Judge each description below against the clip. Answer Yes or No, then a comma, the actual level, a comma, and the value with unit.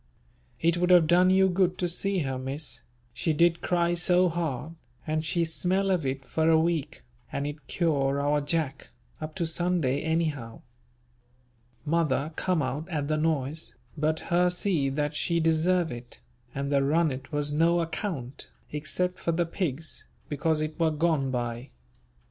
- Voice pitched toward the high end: No, medium, 160 Hz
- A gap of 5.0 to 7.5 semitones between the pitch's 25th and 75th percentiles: No, average, 3.2 semitones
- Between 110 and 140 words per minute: No, average, 160 wpm